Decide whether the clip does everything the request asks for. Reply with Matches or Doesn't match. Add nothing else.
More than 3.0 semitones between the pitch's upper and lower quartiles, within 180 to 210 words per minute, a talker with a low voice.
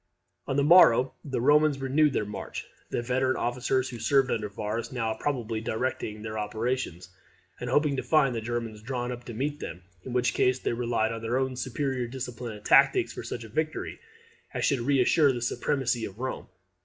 Doesn't match